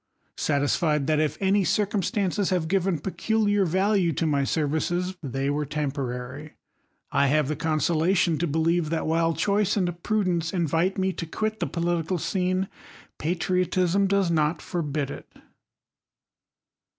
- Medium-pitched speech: Yes, medium, 170 Hz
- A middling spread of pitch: Yes, average, 3.7 semitones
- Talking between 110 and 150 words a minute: Yes, average, 140 wpm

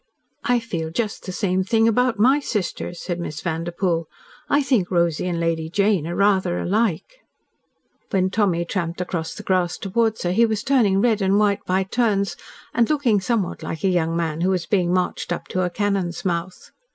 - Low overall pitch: No, high, 190 Hz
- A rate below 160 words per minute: No, average, 190 wpm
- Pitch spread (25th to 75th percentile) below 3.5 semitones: No, average, 3.8 semitones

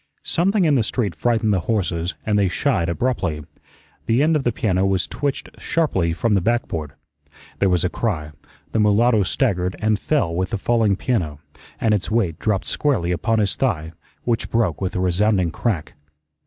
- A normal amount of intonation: Yes, average, 4.8 semitones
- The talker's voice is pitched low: Yes, low, 105 Hz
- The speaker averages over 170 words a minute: Yes, average, 180 wpm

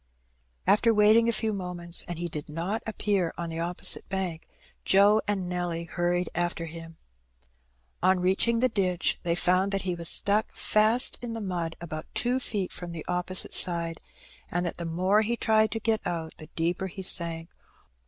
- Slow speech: No, average, 185 wpm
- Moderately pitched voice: Yes, medium, 180 Hz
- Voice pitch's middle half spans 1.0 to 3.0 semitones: No, average, 3.5 semitones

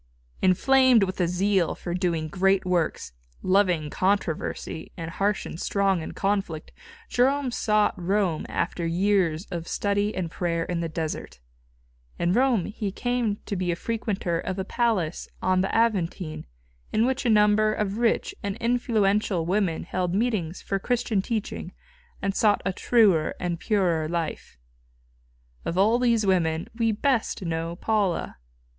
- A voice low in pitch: No, high, 195 Hz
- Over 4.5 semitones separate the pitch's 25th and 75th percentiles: No, average, 3.9 semitones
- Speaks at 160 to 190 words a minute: No, average, 150 wpm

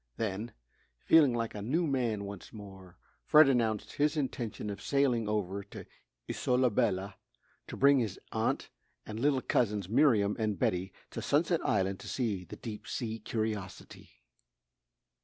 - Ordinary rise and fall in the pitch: Yes, average, 4.2 semitones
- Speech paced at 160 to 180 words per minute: No, average, 145 wpm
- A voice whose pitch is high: No, low, 110 Hz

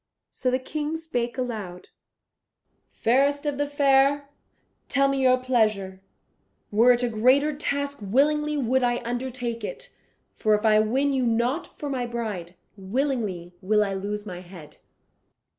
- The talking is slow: No, average, 145 wpm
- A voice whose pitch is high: Yes, high, 245 Hz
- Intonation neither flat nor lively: Yes, average, 4.7 semitones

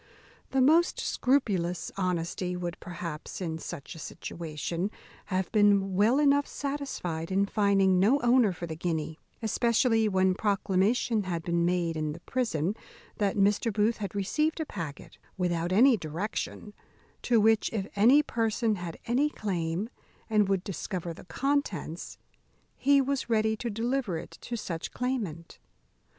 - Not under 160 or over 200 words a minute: No, average, 145 wpm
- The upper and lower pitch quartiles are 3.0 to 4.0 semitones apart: No, average, 5.2 semitones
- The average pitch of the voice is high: Yes, high, 200 Hz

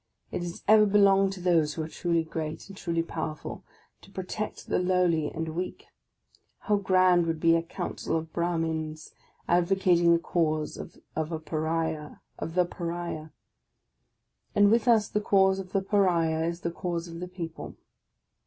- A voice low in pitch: No, medium, 170 Hz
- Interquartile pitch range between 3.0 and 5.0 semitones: No, narrow, 2.6 semitones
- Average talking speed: Yes, average, 155 wpm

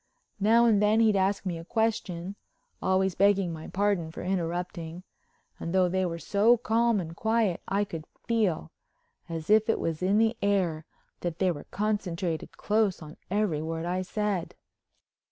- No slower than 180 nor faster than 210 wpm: No, average, 155 wpm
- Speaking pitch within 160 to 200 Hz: Yes, high, 190 Hz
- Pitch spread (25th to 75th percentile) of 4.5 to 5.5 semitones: No, average, 3.8 semitones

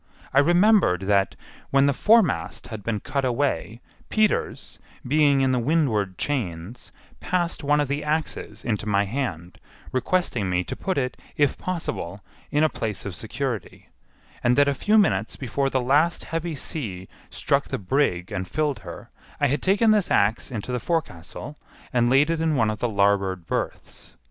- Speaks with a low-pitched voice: Yes, low, 130 Hz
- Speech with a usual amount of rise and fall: No, wide, 6.6 semitones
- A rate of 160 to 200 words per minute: Yes, average, 170 wpm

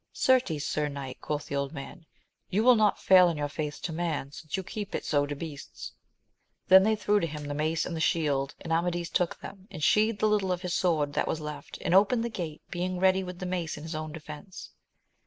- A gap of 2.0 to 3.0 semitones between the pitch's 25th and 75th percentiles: No, average, 4.0 semitones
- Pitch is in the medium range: Yes, medium, 165 Hz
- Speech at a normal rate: No, fast, 230 wpm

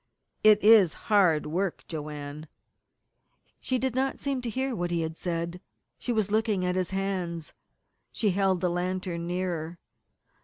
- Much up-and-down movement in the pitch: No, average, 4.0 semitones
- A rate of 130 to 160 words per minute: Yes, average, 150 wpm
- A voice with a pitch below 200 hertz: Yes, medium, 185 Hz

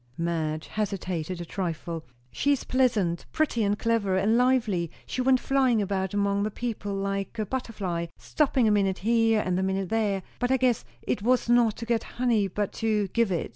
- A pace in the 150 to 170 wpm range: No, average, 190 wpm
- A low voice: No, high, 210 Hz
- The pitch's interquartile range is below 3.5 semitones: No, average, 3.8 semitones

